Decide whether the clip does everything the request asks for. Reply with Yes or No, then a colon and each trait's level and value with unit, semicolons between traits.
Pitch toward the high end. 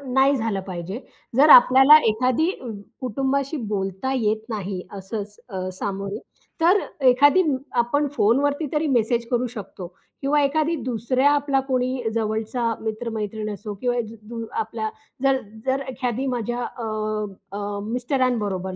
Yes: high, 240 Hz